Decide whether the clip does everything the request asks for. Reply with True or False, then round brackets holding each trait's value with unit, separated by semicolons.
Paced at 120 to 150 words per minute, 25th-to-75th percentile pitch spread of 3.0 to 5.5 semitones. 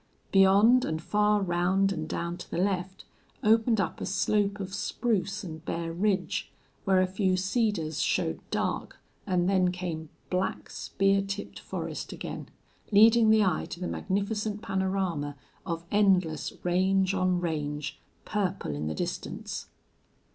False (140 wpm; 2.6 semitones)